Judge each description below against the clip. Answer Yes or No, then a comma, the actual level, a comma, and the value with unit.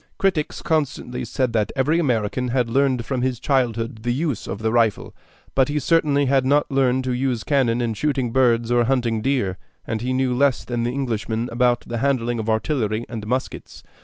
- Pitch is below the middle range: Yes, low, 125 Hz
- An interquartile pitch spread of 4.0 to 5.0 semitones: No, average, 2.8 semitones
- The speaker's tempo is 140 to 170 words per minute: No, average, 190 wpm